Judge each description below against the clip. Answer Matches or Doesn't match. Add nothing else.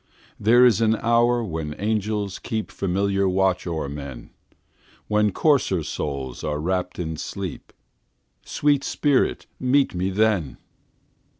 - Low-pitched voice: Matches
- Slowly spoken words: Matches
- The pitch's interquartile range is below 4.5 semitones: Doesn't match